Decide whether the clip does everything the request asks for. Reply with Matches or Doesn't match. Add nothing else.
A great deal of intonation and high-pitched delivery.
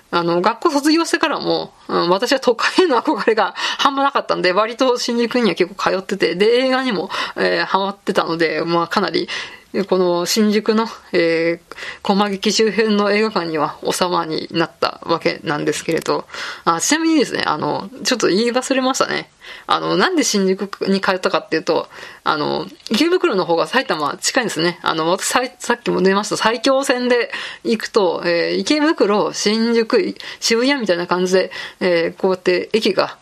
Matches